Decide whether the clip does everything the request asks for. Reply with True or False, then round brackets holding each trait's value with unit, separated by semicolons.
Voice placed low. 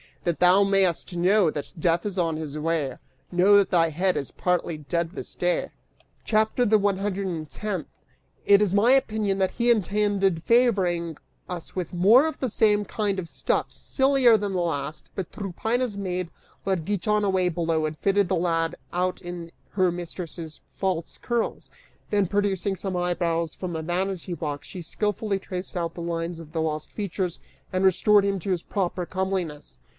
False (185 Hz)